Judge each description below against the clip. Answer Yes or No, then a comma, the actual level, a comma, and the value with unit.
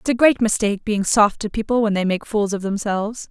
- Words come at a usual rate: No, fast, 255 wpm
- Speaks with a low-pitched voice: No, high, 210 Hz